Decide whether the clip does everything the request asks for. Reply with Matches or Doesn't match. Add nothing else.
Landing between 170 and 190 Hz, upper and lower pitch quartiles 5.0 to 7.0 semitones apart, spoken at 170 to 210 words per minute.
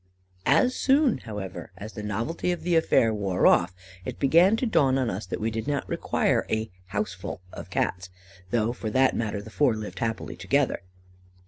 Doesn't match